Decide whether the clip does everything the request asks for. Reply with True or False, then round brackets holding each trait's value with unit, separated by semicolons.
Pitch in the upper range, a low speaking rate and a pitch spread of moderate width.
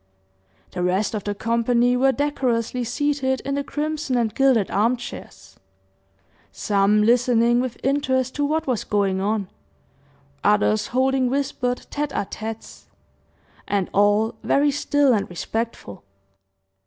True (245 Hz; 130 wpm; 4.2 semitones)